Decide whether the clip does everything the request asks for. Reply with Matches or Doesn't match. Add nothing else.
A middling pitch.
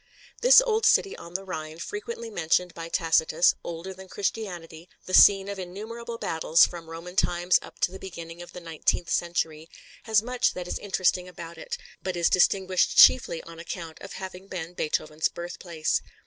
Matches